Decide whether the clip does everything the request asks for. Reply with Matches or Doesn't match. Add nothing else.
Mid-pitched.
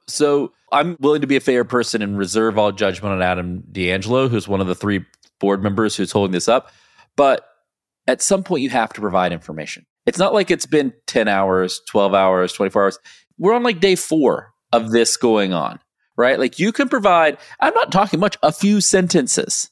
Doesn't match